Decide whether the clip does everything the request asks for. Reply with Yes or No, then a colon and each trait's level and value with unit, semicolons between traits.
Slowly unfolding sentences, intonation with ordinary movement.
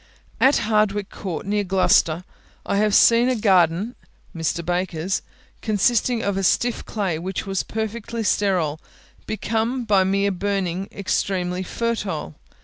Yes: slow, 130 wpm; average, 3.3 semitones